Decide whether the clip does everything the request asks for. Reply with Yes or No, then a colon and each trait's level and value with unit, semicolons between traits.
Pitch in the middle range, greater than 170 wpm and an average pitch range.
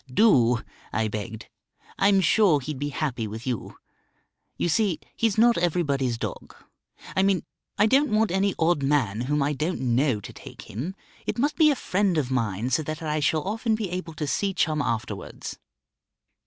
No: medium, 155 Hz; average, 180 wpm; wide, 7.3 semitones